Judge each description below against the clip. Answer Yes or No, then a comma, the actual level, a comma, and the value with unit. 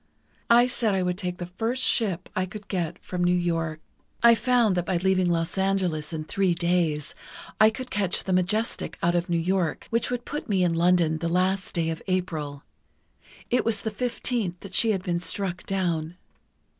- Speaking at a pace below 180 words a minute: No, average, 195 wpm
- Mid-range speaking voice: Yes, medium, 180 Hz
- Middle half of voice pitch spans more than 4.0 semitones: No, average, 3.1 semitones